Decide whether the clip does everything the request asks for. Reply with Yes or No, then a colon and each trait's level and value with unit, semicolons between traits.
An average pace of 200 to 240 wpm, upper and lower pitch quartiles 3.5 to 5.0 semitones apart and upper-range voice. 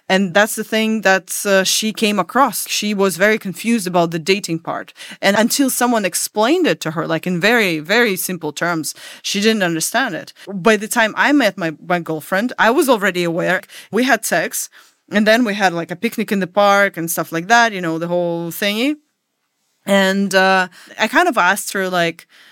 Yes: fast, 205 wpm; average, 3.9 semitones; high, 195 Hz